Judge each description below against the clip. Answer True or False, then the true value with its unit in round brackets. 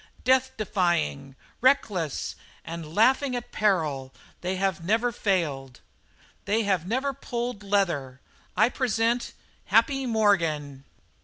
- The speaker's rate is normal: False (105 wpm)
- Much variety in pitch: True (6.8 semitones)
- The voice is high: True (200 Hz)